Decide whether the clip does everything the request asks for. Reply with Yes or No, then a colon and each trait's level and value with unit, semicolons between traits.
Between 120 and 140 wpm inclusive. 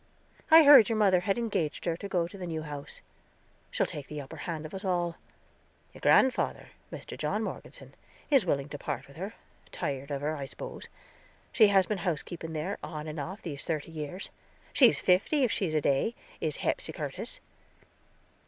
No: average, 190 wpm